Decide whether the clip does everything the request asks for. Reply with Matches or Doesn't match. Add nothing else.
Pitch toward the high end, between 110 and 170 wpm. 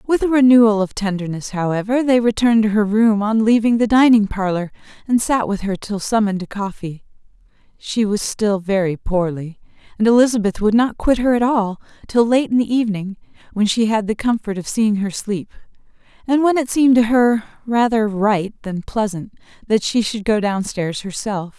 Doesn't match